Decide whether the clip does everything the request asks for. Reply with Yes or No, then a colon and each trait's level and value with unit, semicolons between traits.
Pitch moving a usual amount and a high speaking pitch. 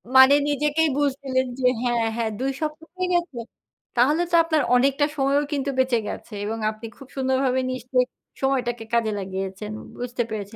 Yes: average, 3.2 semitones; very high, 260 Hz